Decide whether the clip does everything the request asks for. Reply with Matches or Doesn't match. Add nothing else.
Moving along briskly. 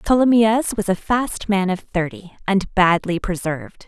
Doesn't match